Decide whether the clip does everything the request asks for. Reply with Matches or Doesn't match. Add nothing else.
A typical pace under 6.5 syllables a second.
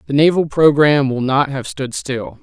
Matches